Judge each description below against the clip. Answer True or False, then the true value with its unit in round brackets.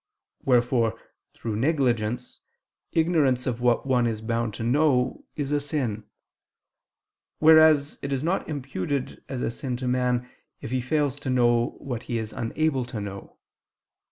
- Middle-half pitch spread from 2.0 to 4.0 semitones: True (3.3 semitones)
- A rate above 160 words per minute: False (150 wpm)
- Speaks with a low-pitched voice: True (125 Hz)